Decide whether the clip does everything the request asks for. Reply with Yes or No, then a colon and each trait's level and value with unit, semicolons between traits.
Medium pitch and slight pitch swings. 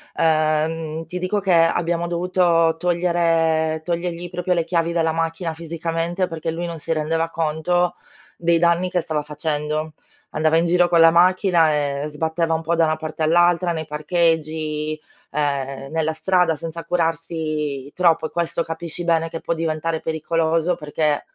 Yes: medium, 165 Hz; narrow, 1.5 semitones